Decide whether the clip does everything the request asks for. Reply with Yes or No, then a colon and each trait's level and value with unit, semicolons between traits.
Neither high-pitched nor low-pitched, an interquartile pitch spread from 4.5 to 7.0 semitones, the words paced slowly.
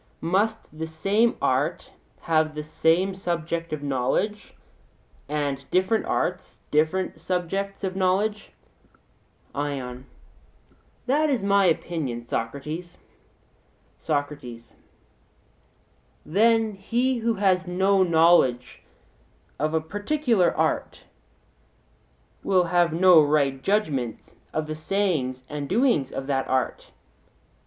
Yes: medium, 170 Hz; average, 5.2 semitones; slow, 100 wpm